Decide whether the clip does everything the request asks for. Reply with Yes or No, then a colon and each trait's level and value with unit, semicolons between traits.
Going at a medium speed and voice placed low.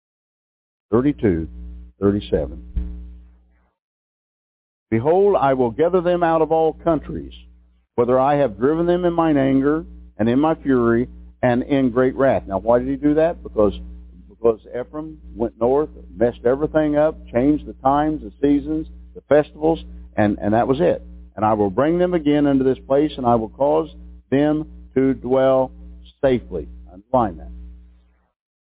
Yes: average, 150 wpm; low, 120 Hz